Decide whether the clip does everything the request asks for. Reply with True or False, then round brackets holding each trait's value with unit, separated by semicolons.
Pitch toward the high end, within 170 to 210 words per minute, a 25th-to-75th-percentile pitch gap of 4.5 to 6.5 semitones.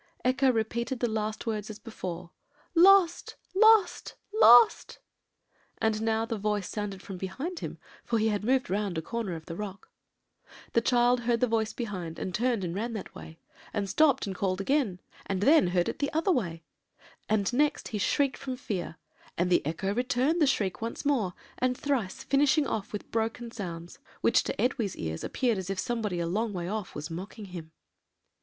True (220 Hz; 185 wpm; 4.9 semitones)